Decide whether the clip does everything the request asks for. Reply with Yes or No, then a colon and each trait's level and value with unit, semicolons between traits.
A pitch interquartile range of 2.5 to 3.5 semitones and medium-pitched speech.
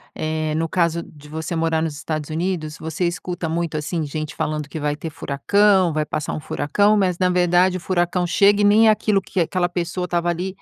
Yes: average, 2.8 semitones; medium, 170 Hz